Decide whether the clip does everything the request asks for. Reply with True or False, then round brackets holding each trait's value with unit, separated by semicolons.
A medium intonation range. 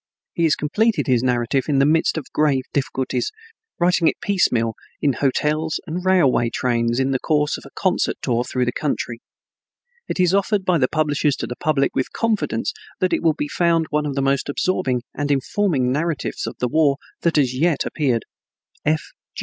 True (4.2 semitones)